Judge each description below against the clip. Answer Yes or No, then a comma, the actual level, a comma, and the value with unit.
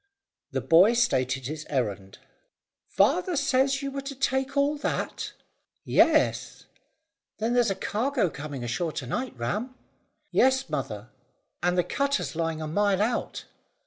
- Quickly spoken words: No, average, 140 wpm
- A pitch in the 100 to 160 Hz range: No, high, 200 Hz